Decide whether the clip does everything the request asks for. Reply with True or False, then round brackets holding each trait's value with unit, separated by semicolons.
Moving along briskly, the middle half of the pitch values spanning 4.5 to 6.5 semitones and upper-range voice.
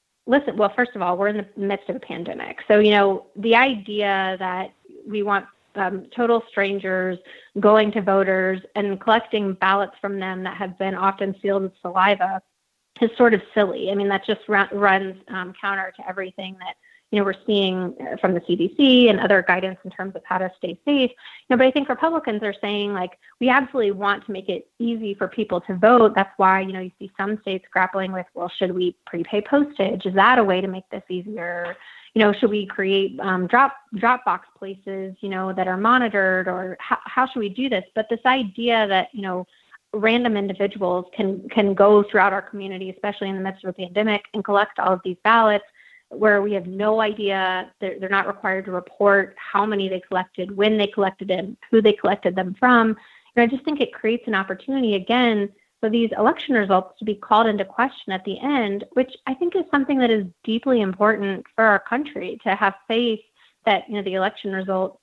False (210 wpm; 2.8 semitones; 200 Hz)